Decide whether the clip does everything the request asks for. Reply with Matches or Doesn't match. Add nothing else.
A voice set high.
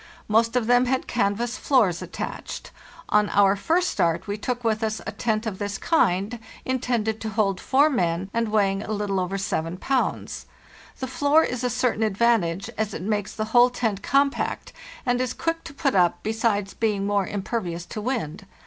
Matches